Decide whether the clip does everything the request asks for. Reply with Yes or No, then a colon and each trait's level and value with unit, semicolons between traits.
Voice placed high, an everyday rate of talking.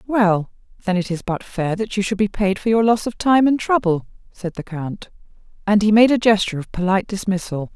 No: high, 200 Hz; fast, 225 wpm